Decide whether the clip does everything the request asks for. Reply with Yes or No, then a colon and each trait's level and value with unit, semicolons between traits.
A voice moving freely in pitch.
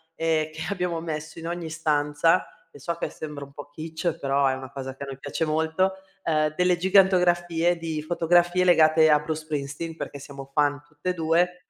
No: average, 2.8 semitones